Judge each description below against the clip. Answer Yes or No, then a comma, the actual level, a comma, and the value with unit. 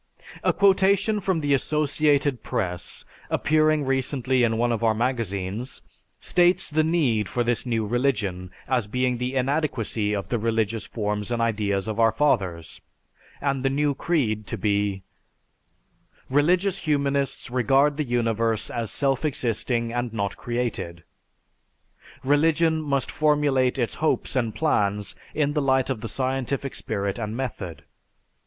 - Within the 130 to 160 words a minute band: Yes, average, 140 wpm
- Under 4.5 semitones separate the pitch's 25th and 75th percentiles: No, average, 4.8 semitones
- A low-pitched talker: Yes, low, 125 Hz